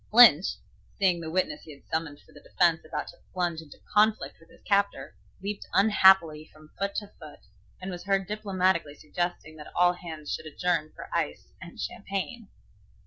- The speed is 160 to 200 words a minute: Yes, average, 175 wpm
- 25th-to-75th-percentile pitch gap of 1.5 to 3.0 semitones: No, average, 3.9 semitones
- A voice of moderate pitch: Yes, medium, 180 Hz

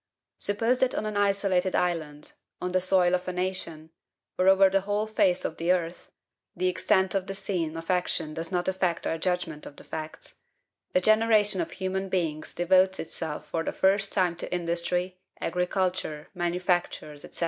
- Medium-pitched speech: Yes, medium, 180 Hz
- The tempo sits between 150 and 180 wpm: Yes, average, 175 wpm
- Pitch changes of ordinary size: No, narrow, 2.2 semitones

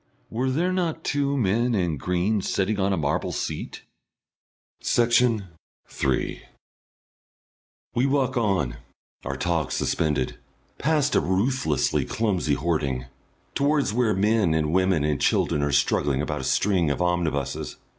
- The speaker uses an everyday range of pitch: No, wide, 7.9 semitones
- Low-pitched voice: Yes, very low, 95 Hz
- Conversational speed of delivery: No, slow, 130 wpm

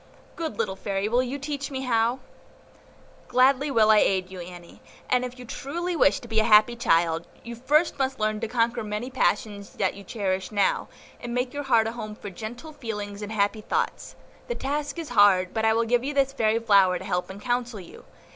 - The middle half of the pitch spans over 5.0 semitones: No, average, 4.0 semitones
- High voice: Yes, high, 225 Hz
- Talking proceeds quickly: Yes, fast, 210 wpm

